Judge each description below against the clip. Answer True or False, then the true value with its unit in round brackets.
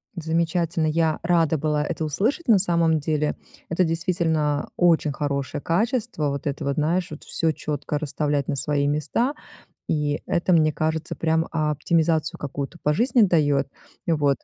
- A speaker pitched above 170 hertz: False (155 Hz)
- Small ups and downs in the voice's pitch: True (2.3 semitones)